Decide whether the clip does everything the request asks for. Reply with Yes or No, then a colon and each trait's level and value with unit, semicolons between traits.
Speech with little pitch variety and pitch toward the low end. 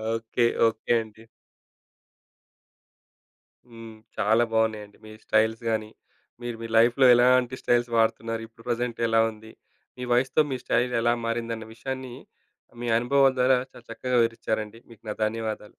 Yes: narrow, 1.6 semitones; low, 115 Hz